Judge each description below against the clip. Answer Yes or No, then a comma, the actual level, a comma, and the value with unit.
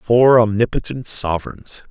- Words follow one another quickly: No, slow, 95 wpm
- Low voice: Yes, low, 110 Hz